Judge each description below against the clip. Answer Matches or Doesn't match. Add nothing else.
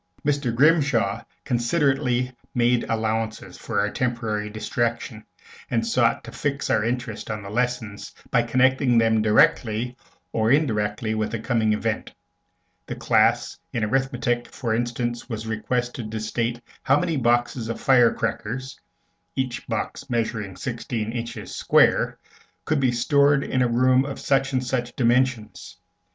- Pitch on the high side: Doesn't match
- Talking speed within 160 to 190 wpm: Doesn't match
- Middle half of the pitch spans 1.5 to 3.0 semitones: Matches